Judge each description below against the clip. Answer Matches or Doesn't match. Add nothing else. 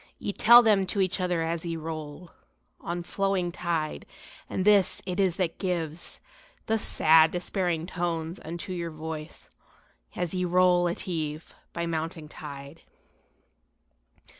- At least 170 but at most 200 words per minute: Doesn't match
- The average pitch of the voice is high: Doesn't match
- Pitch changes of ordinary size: Doesn't match